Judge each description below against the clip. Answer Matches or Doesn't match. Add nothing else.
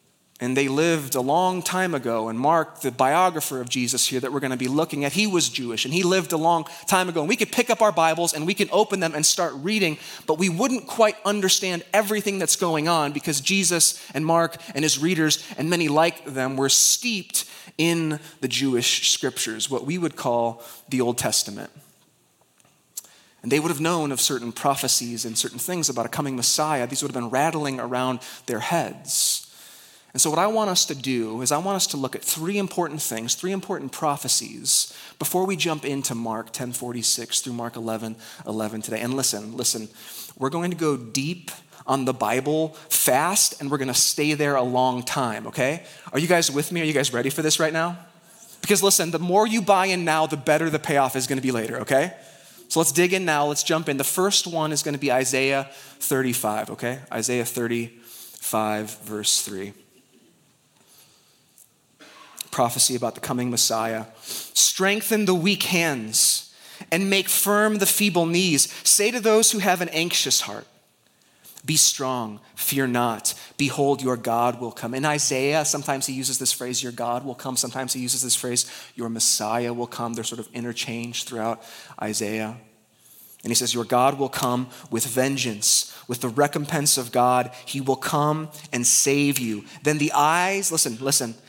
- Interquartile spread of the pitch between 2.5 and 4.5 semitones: Doesn't match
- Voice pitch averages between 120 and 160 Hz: Matches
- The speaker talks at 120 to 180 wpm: Doesn't match